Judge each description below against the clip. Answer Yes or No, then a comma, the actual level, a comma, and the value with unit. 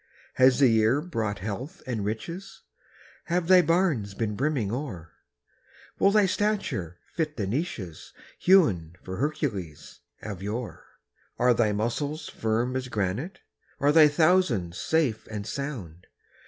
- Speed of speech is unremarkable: No, slow, 130 wpm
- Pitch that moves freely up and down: Yes, wide, 7.3 semitones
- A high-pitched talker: No, low, 125 Hz